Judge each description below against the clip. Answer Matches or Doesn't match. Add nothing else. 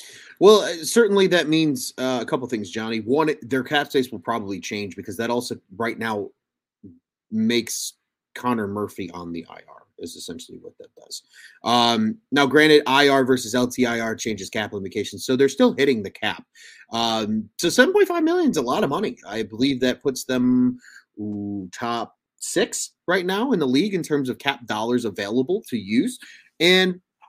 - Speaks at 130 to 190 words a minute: Matches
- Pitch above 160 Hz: Doesn't match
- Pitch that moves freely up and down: Matches